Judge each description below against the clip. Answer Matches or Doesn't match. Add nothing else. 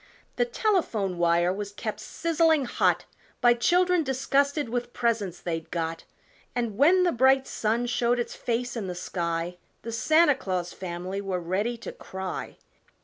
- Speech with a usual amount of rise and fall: Doesn't match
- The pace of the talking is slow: Doesn't match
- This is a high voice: Matches